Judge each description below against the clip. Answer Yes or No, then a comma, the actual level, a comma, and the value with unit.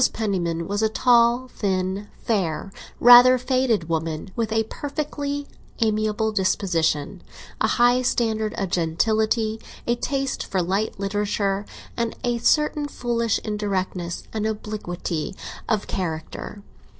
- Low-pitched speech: No, high, 215 Hz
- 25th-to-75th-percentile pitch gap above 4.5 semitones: No, average, 4.0 semitones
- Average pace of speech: No, slow, 115 wpm